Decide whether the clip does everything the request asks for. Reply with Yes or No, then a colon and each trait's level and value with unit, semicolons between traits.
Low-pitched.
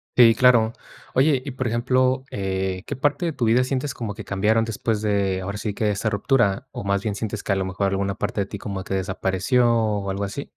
Yes: low, 105 Hz